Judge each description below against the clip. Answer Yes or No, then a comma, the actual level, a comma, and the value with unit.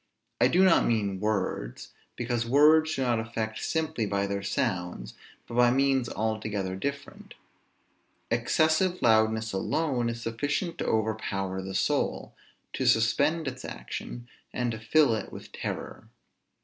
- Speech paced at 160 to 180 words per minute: No, slow, 135 wpm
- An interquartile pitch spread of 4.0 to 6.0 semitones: Yes, average, 4.6 semitones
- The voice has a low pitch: Yes, low, 115 Hz